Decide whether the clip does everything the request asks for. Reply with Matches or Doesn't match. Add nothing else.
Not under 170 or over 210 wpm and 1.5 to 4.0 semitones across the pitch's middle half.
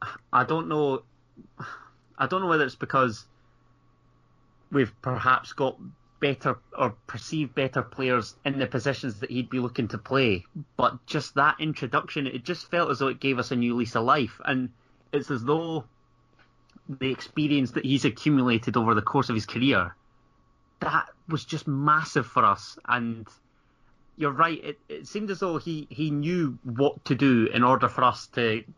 Matches